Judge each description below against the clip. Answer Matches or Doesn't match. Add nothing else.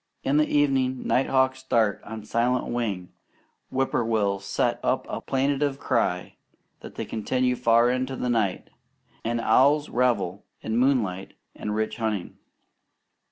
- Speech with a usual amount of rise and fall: Matches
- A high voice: Doesn't match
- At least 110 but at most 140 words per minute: Matches